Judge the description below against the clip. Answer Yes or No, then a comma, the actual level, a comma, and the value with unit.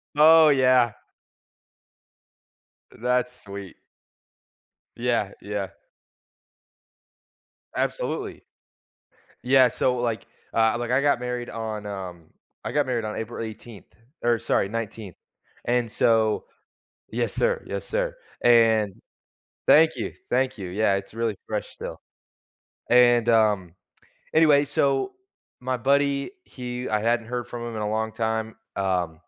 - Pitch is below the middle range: Yes, low, 115 Hz